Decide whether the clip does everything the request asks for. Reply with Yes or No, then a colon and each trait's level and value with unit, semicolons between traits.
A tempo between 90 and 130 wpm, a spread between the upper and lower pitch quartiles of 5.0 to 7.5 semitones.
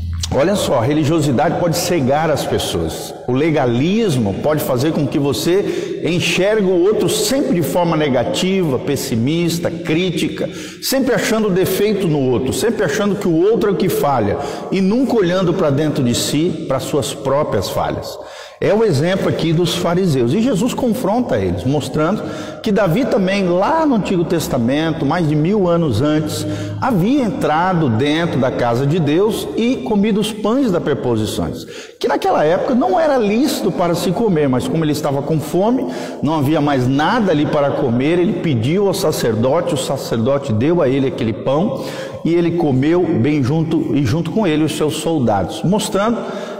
No: average, 170 wpm; wide, 5.4 semitones